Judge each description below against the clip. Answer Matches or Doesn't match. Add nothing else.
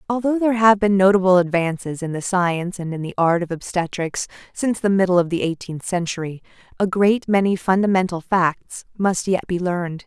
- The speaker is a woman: Matches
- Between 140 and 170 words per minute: Doesn't match